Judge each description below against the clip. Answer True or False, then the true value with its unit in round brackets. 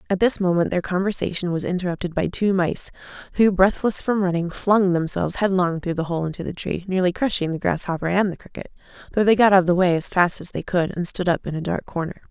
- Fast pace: True (240 wpm)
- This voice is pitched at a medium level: True (180 Hz)